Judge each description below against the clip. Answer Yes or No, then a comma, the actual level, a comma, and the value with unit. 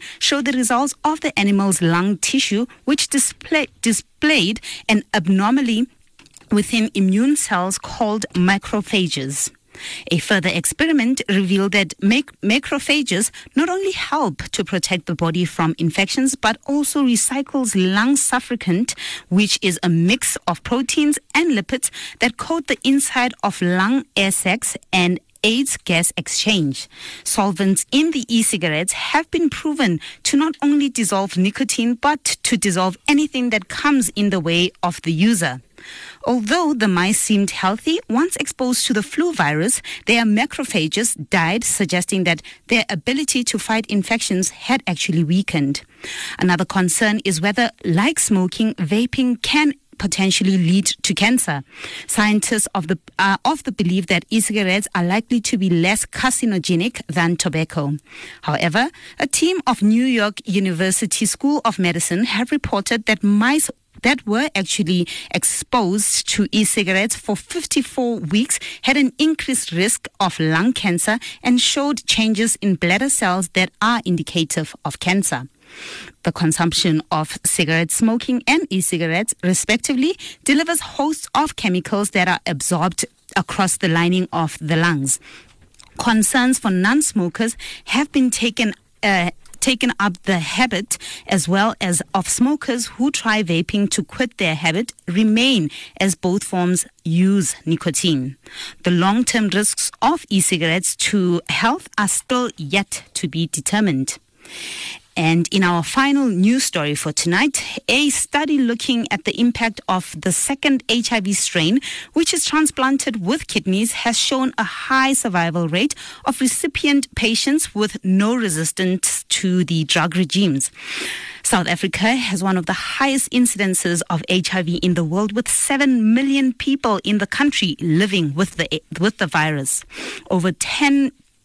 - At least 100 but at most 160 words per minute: Yes, average, 145 wpm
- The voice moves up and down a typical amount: No, wide, 5.8 semitones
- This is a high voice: Yes, high, 210 Hz